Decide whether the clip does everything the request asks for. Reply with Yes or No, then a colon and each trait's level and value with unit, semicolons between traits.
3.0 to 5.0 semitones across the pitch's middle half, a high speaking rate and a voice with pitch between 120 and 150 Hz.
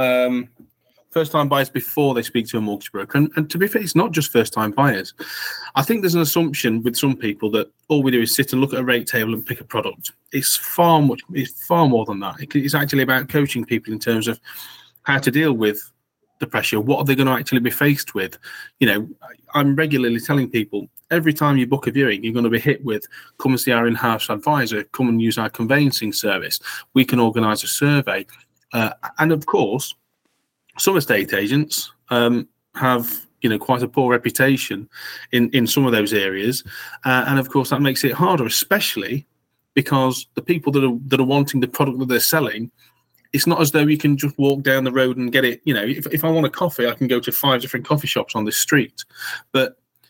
Yes: average, 3.4 semitones; fast, 225 wpm; low, 130 Hz